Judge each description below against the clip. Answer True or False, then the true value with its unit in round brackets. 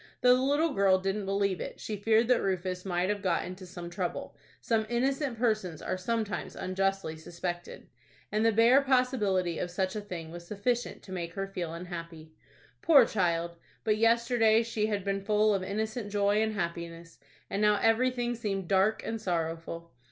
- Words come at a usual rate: True (170 wpm)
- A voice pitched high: True (200 Hz)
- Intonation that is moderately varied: True (4.0 semitones)